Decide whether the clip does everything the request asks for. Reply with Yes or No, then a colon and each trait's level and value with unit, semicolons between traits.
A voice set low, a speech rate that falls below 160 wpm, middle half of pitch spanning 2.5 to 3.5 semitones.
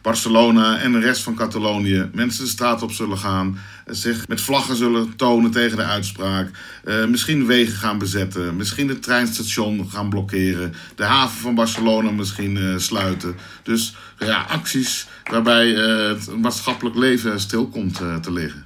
Yes: low, 110 Hz; average, 150 wpm; average, 3.2 semitones